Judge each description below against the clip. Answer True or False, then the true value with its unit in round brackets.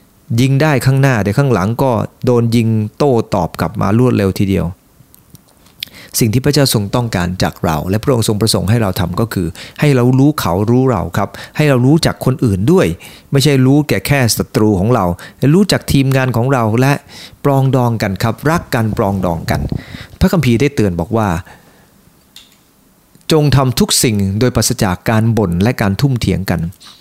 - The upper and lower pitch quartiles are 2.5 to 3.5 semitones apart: False (5.1 semitones)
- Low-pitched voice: True (115 Hz)